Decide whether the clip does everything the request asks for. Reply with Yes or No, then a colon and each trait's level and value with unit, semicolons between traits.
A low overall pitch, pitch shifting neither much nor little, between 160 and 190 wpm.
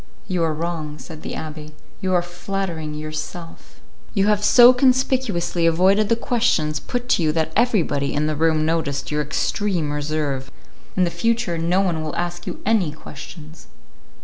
No: medium, 165 Hz; average, 4.2 semitones; average, 165 wpm